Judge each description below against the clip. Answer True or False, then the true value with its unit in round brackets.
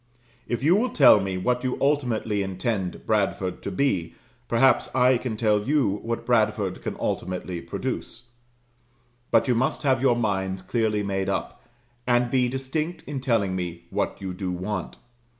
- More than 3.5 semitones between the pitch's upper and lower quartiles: True (4.9 semitones)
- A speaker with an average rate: True (160 wpm)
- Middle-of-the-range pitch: False (110 Hz)